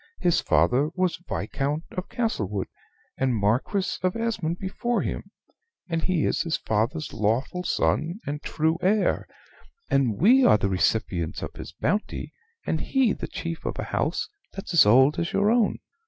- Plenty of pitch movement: Yes, wide, 8.6 semitones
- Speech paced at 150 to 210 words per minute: Yes, average, 160 wpm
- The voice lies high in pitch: No, medium, 160 Hz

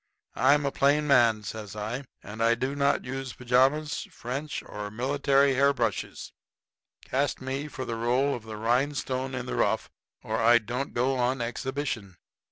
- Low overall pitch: Yes, low, 130 Hz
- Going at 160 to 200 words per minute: Yes, average, 165 wpm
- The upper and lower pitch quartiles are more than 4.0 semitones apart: No, average, 3.2 semitones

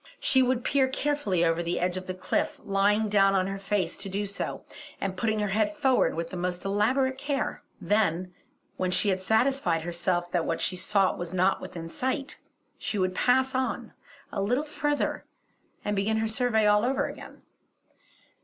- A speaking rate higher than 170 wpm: Yes, average, 180 wpm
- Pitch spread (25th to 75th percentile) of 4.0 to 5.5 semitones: Yes, average, 5.1 semitones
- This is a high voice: Yes, high, 200 Hz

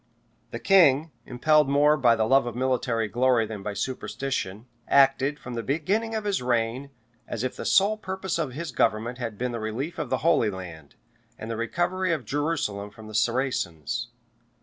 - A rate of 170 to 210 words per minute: Yes, average, 180 wpm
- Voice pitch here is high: No, low, 130 Hz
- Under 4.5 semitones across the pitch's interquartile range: No, average, 5.2 semitones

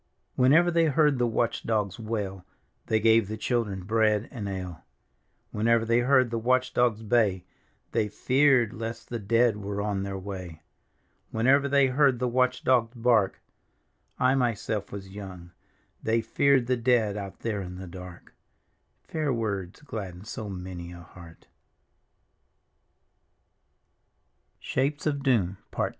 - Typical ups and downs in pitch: Yes, average, 4.0 semitones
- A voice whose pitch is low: Yes, low, 110 Hz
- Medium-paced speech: No, slow, 130 wpm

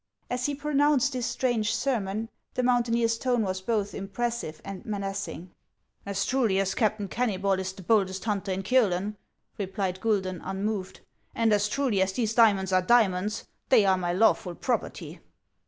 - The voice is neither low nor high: No, high, 210 Hz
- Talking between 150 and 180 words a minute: Yes, average, 165 wpm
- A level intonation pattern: No, average, 3.8 semitones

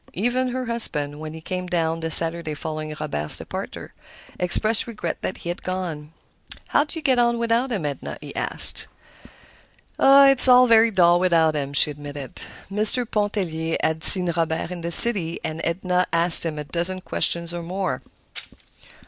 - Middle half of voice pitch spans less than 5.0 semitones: No, wide, 5.5 semitones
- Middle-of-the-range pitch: Yes, medium, 175 Hz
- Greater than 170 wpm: No, average, 165 wpm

